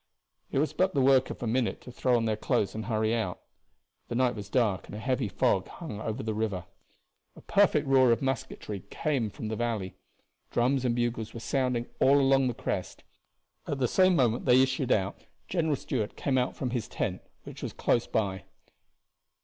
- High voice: No, low, 120 Hz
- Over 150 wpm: Yes, average, 200 wpm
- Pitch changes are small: No, average, 3.3 semitones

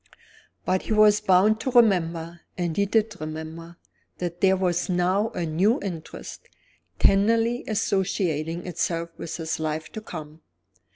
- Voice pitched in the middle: Yes, medium, 180 Hz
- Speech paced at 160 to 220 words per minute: No, slow, 135 wpm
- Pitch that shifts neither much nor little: Yes, average, 4.0 semitones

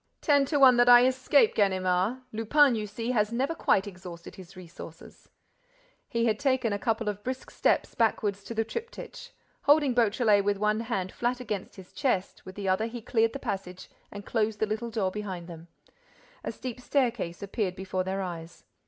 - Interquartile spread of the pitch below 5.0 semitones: Yes, average, 4.3 semitones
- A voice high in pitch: Yes, high, 215 Hz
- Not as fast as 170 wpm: No, average, 185 wpm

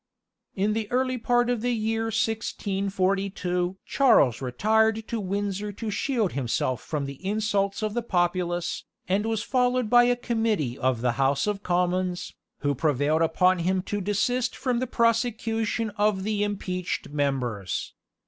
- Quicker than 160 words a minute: No, average, 150 wpm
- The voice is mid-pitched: No, high, 200 Hz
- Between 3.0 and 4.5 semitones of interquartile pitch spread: Yes, average, 4.2 semitones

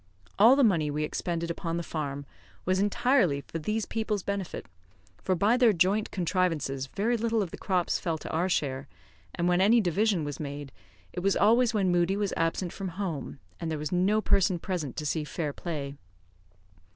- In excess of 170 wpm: Yes, average, 190 wpm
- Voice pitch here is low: No, medium, 180 Hz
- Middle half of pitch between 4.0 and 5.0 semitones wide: Yes, average, 4.5 semitones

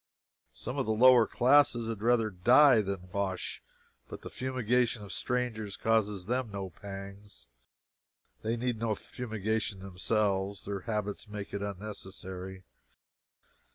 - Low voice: Yes, low, 105 Hz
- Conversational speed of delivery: No, slow, 125 wpm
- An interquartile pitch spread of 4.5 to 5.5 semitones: No, average, 3.1 semitones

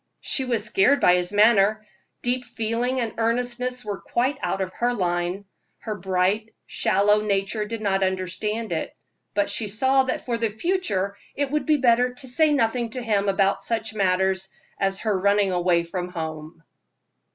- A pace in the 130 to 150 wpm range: No, average, 170 wpm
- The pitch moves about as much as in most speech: Yes, average, 4.1 semitones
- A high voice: Yes, high, 215 Hz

